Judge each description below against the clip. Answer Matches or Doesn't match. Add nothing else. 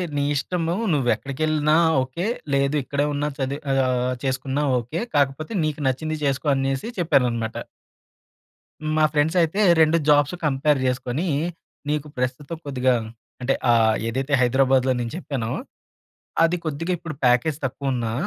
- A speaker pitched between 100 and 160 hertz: Matches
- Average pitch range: Matches